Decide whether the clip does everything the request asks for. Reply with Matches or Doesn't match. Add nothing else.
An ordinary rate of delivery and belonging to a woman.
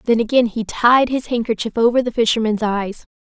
Matches